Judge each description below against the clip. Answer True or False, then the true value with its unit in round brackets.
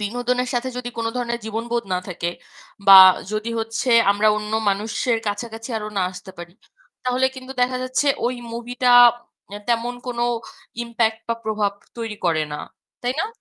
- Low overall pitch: False (230 Hz)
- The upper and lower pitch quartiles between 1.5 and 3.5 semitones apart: True (2.7 semitones)